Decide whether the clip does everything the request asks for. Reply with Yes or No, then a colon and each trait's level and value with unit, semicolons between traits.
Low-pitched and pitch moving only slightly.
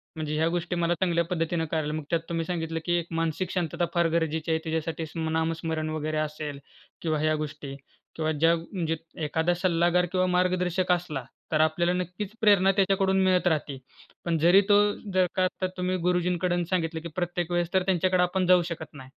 No: medium, 170 Hz; narrow, 2.1 semitones